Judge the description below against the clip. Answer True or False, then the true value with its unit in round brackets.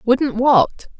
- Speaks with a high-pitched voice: True (245 Hz)